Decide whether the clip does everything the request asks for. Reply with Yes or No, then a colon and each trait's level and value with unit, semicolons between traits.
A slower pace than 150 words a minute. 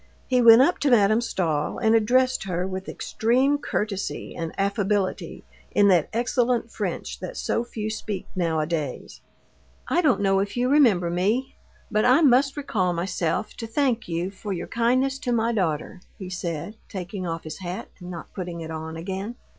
No: average, 170 wpm